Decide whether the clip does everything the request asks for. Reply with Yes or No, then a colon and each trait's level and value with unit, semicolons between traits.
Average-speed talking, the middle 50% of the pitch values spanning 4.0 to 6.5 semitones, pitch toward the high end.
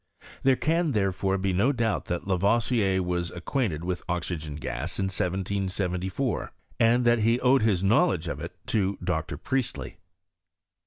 No: average, 160 wpm; average, 4.7 semitones; very low, 95 Hz